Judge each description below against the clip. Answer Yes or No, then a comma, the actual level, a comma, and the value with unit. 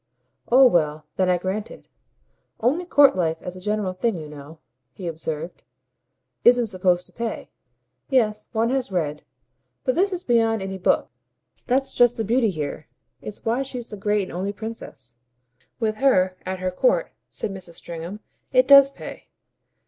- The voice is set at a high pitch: Yes, high, 210 Hz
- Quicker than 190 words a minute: No, average, 165 wpm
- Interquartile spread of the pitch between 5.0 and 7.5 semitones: Yes, average, 5.3 semitones